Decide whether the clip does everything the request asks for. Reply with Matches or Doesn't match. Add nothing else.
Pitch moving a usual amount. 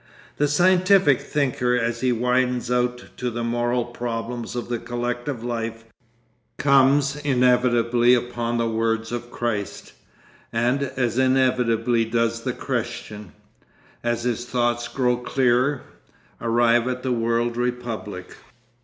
Doesn't match